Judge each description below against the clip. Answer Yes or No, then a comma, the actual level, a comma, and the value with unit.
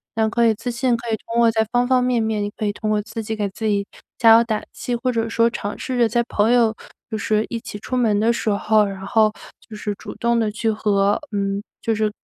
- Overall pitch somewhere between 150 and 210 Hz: No, high, 220 Hz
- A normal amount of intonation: No, narrow, 1.9 semitones